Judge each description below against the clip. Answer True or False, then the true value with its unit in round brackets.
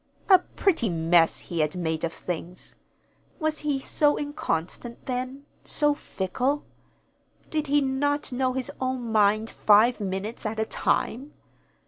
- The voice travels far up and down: True (7.1 semitones)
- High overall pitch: True (250 Hz)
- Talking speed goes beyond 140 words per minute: False (135 wpm)